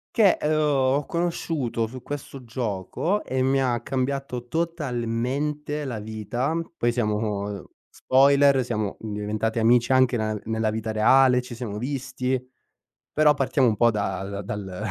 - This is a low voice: Yes, low, 125 Hz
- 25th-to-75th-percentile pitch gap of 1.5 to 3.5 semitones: No, average, 4.0 semitones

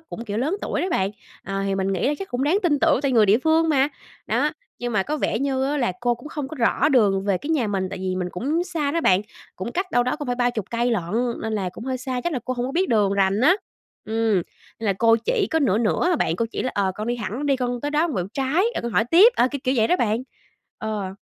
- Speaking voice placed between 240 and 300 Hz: Yes, high, 245 Hz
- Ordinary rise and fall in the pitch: No, wide, 5.7 semitones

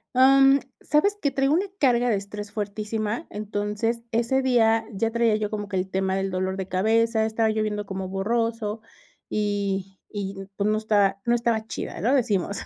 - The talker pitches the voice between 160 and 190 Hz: No, high, 215 Hz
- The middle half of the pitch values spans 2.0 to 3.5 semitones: Yes, narrow, 2.6 semitones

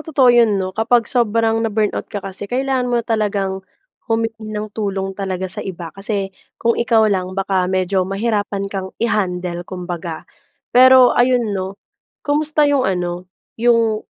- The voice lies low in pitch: No, high, 210 Hz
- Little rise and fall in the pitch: No, average, 3.7 semitones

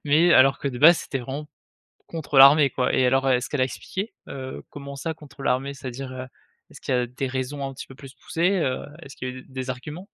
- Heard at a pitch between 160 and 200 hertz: No, low, 135 Hz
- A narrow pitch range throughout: Yes, narrow, 2.2 semitones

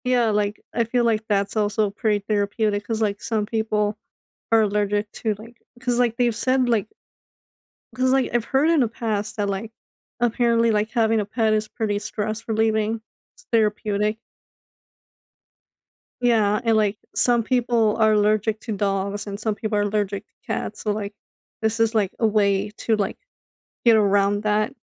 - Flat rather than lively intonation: Yes, narrow, 1.8 semitones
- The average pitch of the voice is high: Yes, high, 215 Hz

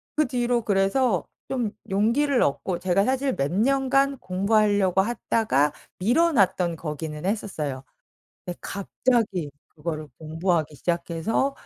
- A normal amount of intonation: No, wide, 6.4 semitones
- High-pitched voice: Yes, high, 195 Hz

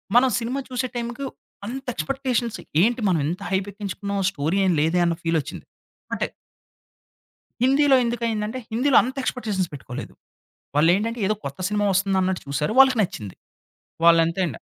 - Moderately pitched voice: No, high, 205 Hz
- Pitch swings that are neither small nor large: No, wide, 6.0 semitones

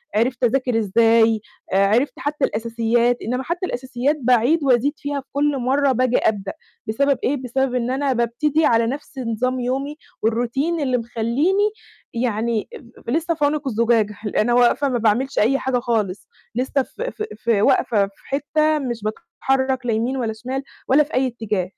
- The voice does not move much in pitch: No, average, 3.2 semitones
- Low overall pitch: No, very high, 250 Hz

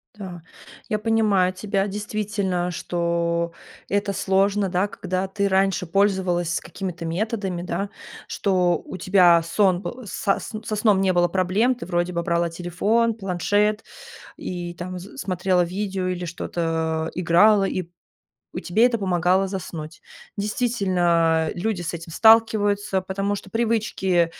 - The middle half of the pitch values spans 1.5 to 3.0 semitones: Yes, average, 2.7 semitones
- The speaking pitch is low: No, high, 190 Hz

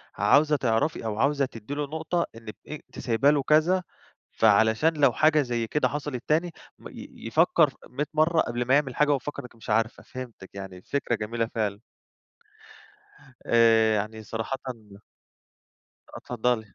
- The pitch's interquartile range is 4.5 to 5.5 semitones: Yes, average, 4.9 semitones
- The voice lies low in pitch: Yes, low, 125 Hz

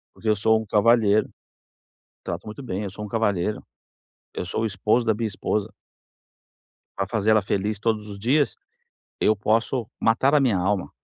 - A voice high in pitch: No, low, 110 Hz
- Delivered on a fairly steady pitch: Yes, narrow, 2.0 semitones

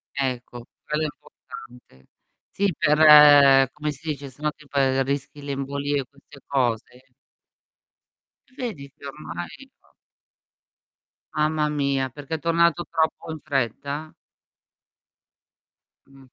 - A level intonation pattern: Yes, narrow, 2.1 semitones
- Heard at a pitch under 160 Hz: Yes, medium, 140 Hz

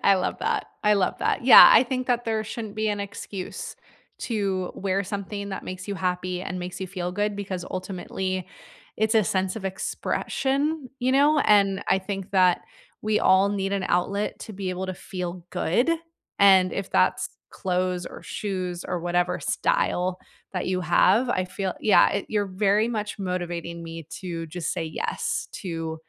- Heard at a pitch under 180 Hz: No, high, 190 Hz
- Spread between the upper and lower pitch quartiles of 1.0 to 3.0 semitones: Yes, narrow, 2.4 semitones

